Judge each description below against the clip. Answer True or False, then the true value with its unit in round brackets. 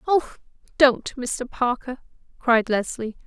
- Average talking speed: False (110 wpm)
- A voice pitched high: True (255 Hz)